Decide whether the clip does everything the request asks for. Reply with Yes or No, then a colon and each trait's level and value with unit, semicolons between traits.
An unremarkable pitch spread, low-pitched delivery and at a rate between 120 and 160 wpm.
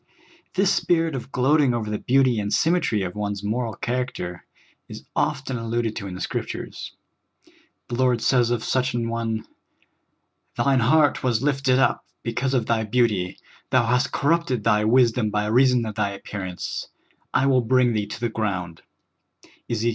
No: average, 3.3 semitones; low, 120 Hz; average, 170 wpm